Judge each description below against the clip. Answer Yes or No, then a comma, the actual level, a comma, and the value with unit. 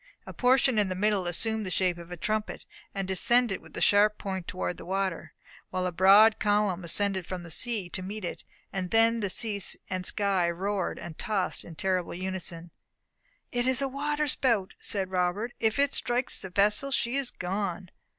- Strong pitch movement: No, average, 3.5 semitones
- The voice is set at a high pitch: Yes, high, 195 Hz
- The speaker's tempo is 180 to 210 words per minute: Yes, average, 190 wpm